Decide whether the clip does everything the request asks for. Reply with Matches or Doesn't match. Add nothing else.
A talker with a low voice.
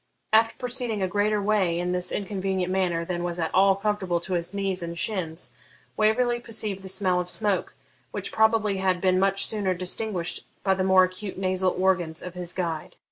Doesn't match